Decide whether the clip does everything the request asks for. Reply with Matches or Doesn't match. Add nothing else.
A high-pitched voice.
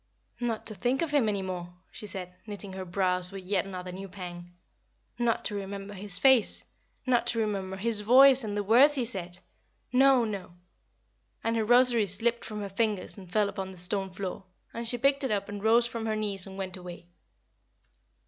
Matches